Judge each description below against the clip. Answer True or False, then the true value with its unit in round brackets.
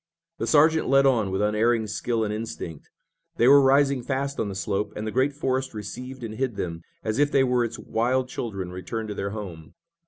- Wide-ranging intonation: False (4.1 semitones)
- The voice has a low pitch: True (115 Hz)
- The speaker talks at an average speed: False (210 wpm)